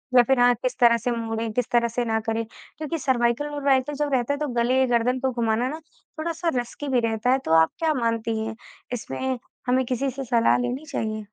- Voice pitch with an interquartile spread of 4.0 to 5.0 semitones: No, average, 2.7 semitones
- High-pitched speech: Yes, high, 245 Hz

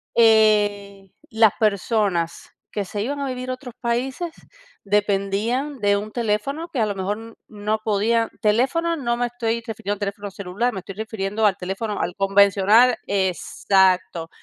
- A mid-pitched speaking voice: No, high, 210 Hz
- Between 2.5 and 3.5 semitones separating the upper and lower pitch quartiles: Yes, average, 3.0 semitones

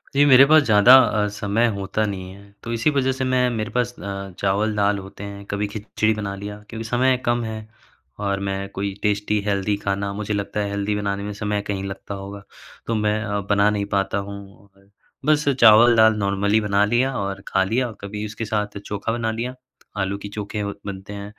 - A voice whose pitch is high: No, low, 105 Hz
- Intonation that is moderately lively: No, narrow, 1.9 semitones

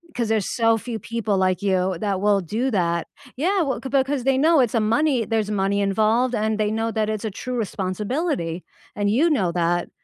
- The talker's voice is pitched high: Yes, high, 215 Hz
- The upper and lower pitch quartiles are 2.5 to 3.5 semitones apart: No, average, 4.3 semitones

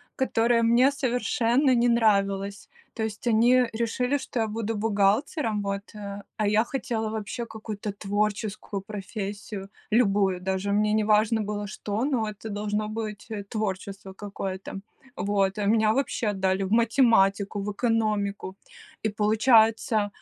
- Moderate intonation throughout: No, narrow, 2.1 semitones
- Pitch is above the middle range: Yes, high, 215 Hz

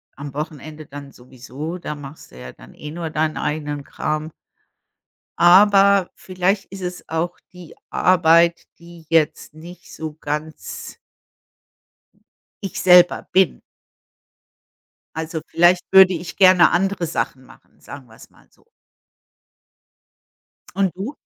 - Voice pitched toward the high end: No, medium, 165 Hz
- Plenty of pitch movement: No, average, 3.2 semitones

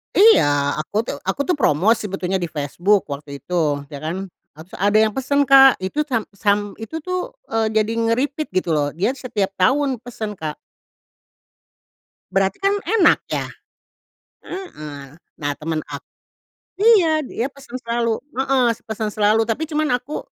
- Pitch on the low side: No, high, 220 Hz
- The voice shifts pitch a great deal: Yes, wide, 7.4 semitones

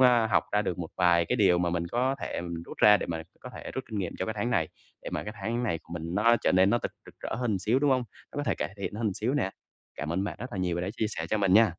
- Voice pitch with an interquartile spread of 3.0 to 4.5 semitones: No, average, 5.2 semitones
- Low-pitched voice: Yes, low, 100 Hz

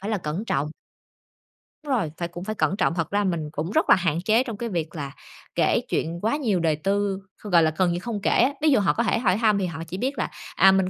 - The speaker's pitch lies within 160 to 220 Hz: Yes, high, 190 Hz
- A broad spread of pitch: No, average, 4.4 semitones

